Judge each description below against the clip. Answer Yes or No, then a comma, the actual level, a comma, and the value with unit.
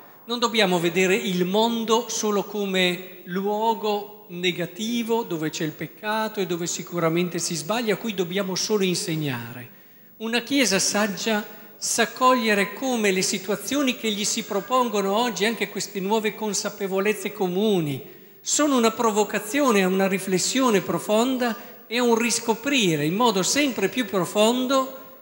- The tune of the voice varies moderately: Yes, average, 3.4 semitones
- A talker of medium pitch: No, high, 210 Hz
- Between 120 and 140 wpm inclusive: Yes, average, 135 wpm